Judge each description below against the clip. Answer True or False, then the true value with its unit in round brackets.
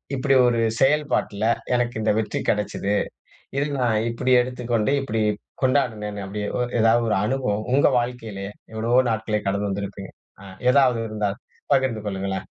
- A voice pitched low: True (110 Hz)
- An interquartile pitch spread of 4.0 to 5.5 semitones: False (3.4 semitones)